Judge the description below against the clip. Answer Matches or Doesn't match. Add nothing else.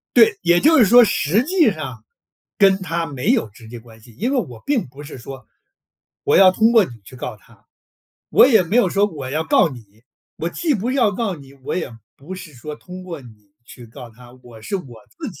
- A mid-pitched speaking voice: Matches